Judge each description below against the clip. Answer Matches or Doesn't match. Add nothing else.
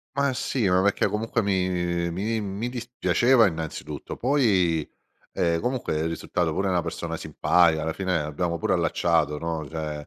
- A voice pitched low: Matches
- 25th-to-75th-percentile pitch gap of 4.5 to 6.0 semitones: Matches